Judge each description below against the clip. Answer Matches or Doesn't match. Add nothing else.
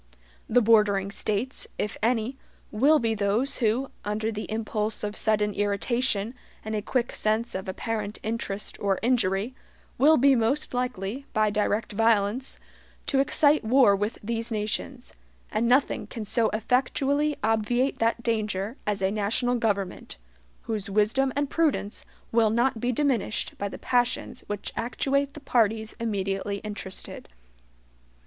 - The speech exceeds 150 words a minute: Doesn't match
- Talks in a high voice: Matches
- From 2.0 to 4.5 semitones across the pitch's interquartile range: Matches